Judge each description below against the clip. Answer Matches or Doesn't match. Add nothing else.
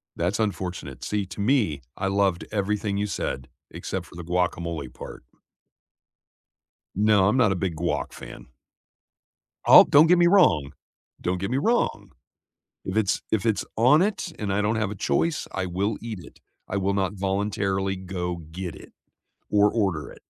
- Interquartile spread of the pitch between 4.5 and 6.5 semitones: Doesn't match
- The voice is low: Matches